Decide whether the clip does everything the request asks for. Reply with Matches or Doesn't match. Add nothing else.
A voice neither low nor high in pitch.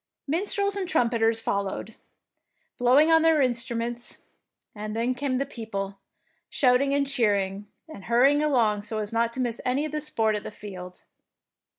Doesn't match